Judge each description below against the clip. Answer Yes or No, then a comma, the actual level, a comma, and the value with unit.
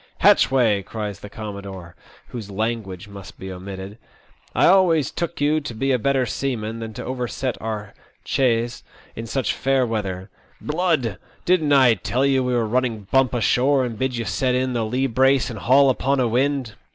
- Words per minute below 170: No, average, 185 wpm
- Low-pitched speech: Yes, low, 120 Hz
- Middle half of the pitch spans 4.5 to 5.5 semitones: No, average, 3.8 semitones